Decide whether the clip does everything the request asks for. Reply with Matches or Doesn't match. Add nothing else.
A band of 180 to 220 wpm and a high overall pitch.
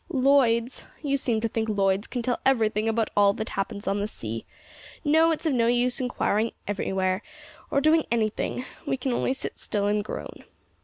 Matches